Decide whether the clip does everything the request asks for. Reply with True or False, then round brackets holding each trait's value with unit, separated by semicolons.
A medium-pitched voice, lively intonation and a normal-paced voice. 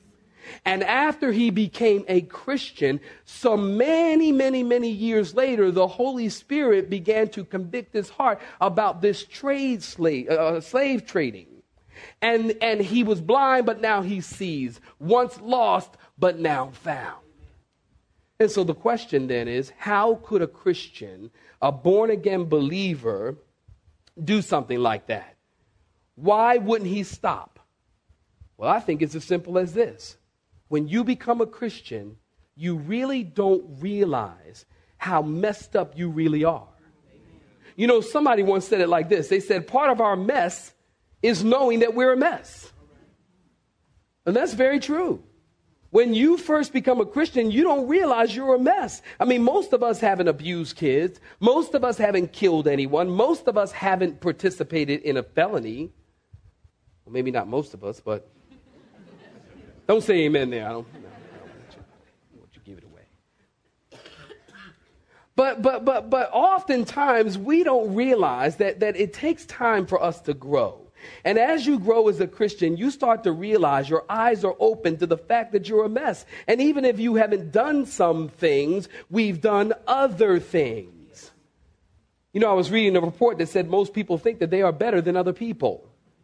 False (215 Hz; 6.4 semitones; 165 wpm)